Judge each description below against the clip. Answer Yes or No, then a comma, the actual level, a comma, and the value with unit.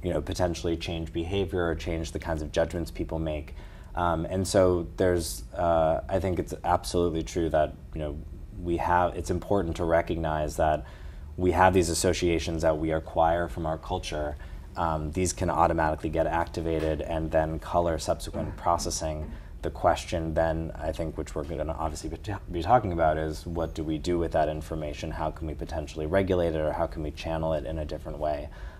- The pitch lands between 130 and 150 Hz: No, very low, 80 Hz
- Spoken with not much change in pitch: Yes, narrow, 1.8 semitones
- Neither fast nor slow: Yes, average, 190 wpm